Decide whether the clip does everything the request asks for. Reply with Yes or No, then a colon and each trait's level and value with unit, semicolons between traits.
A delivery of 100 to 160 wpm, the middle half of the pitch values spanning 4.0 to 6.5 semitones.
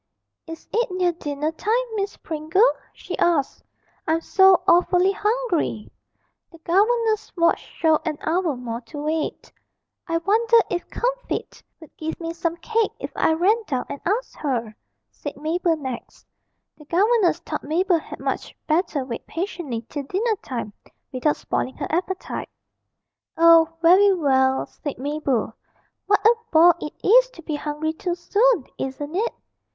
Yes: average, 150 wpm; average, 4.6 semitones